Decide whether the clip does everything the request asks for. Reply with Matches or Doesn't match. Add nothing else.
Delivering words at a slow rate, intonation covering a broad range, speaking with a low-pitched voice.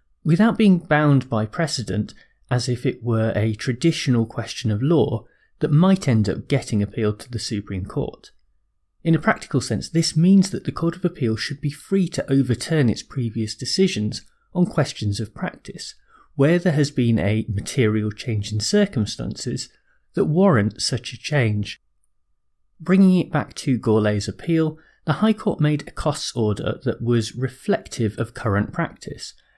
Doesn't match